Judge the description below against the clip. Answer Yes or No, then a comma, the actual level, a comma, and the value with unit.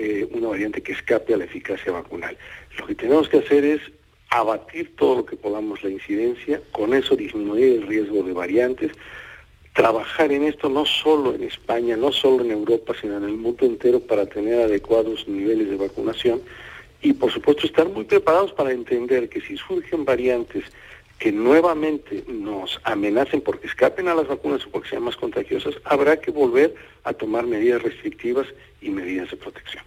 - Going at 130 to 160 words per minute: No, average, 175 wpm